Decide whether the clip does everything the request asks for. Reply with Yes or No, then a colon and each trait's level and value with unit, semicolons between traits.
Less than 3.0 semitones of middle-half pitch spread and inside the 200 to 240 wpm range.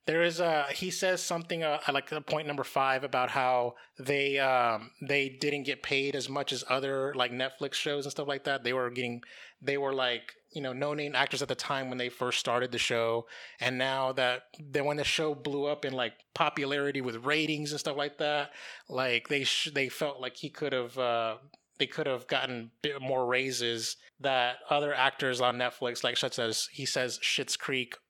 Yes: narrow, 2.5 semitones; fast, 205 wpm